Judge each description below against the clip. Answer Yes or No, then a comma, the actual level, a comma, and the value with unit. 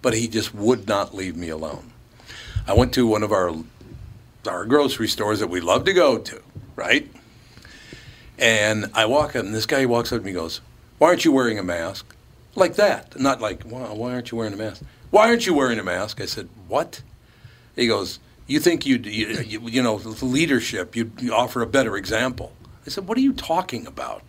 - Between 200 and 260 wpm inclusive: Yes, fast, 205 wpm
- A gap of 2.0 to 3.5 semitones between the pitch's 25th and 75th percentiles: Yes, average, 3.1 semitones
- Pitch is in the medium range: No, low, 115 Hz